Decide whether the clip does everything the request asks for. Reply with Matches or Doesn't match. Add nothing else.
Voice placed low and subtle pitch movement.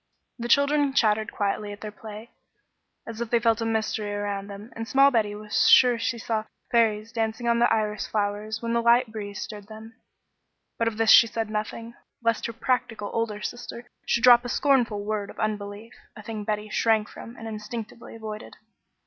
Doesn't match